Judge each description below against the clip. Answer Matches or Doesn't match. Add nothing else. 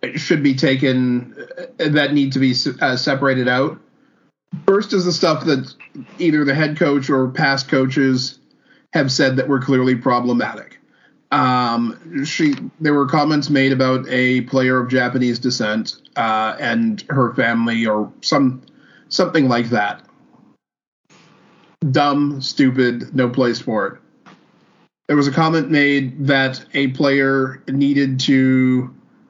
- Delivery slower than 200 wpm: Matches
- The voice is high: Doesn't match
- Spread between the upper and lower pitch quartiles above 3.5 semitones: Doesn't match